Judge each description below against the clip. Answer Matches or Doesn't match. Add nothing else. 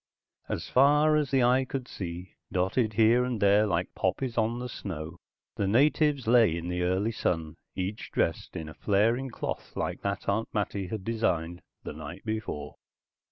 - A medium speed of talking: Matches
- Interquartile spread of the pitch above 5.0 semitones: Matches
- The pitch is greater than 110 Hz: Doesn't match